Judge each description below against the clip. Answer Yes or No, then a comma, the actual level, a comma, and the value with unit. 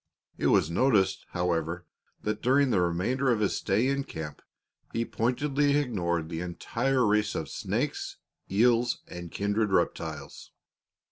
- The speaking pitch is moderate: No, low, 105 Hz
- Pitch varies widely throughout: Yes, wide, 6.2 semitones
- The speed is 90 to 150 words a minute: Yes, slow, 135 wpm